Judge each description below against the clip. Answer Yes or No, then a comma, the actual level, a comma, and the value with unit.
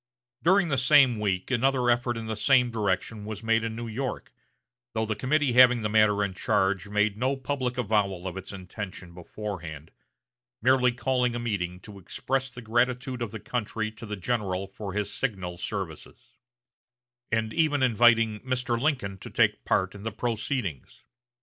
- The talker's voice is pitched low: Yes, low, 110 Hz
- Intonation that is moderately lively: Yes, average, 3.9 semitones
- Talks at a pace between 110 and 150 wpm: No, average, 170 wpm